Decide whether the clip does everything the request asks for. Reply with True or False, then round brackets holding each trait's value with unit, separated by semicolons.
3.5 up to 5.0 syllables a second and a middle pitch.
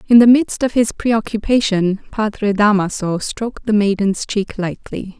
False (4.5 syllables/s; 210 Hz)